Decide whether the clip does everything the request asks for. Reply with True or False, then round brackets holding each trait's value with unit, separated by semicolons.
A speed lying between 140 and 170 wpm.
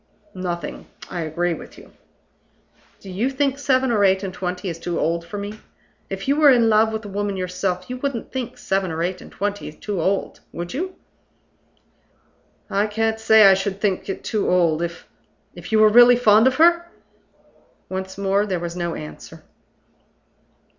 False (180 wpm)